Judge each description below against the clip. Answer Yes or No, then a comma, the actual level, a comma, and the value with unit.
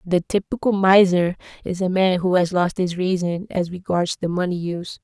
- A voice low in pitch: No, medium, 185 Hz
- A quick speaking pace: No, average, 190 wpm